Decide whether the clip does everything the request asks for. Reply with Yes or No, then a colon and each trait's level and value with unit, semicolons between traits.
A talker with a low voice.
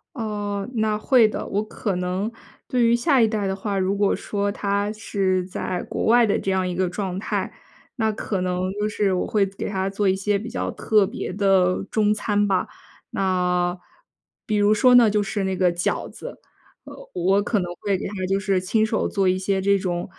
No: high, 200 Hz